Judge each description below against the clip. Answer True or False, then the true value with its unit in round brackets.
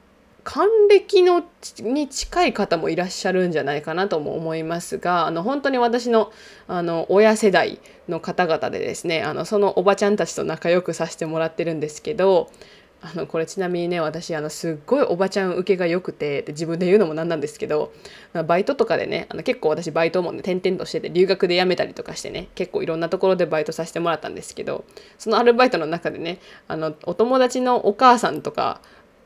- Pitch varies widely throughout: False (4.6 semitones)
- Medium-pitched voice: True (180 Hz)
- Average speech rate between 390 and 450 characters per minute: True (410 characters per minute)